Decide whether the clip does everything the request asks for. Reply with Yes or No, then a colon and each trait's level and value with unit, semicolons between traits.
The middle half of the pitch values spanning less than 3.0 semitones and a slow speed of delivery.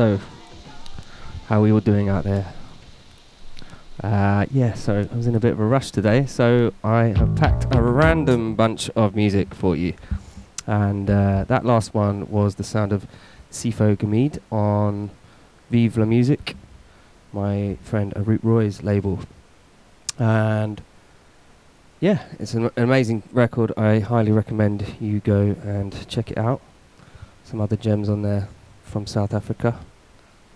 No: narrow, 2.4 semitones; average, 145 wpm